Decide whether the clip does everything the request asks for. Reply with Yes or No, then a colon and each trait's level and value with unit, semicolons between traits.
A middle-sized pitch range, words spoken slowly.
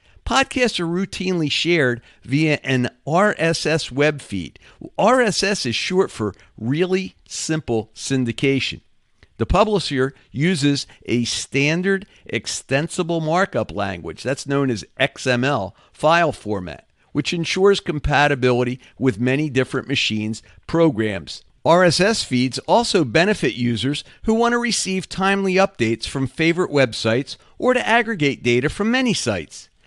No: wide, 7.3 semitones; slow, 120 wpm